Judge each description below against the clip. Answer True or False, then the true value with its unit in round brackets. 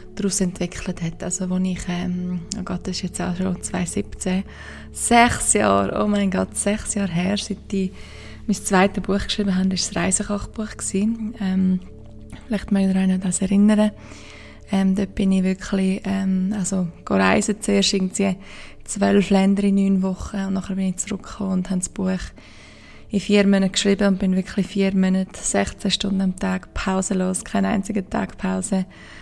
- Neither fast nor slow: True (165 wpm)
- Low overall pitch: False (190 Hz)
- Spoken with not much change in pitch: True (1.5 semitones)